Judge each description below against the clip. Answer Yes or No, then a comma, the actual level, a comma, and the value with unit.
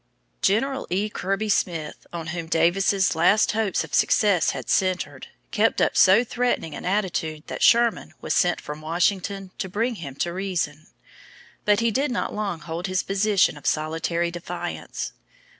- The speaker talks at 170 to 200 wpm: No, average, 160 wpm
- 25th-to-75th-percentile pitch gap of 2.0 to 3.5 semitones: No, average, 3.9 semitones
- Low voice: No, medium, 185 Hz